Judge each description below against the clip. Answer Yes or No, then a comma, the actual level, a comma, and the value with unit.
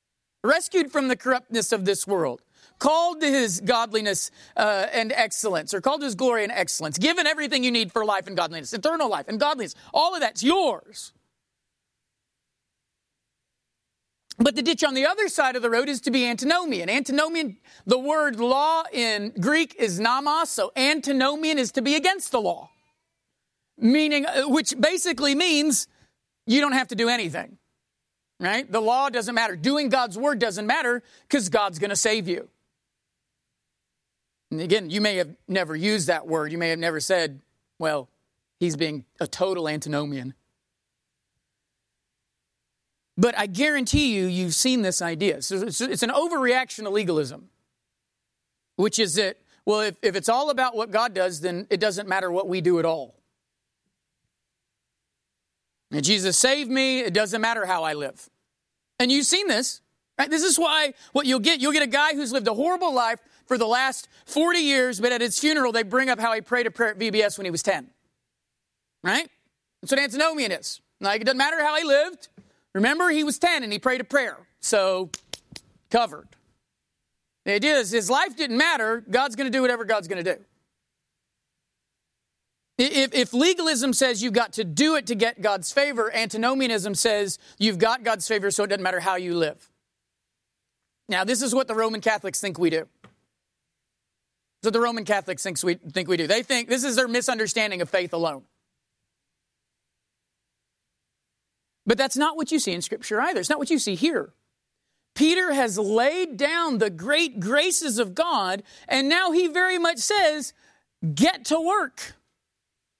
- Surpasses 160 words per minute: Yes, average, 170 wpm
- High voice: Yes, high, 240 Hz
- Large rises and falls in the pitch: Yes, wide, 6.2 semitones